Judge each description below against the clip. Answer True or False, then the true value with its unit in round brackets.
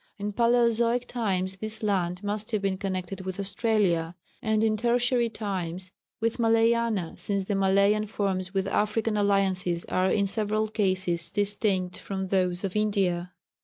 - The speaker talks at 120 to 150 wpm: True (145 wpm)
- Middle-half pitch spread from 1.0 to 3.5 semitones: True (2.6 semitones)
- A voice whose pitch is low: False (200 Hz)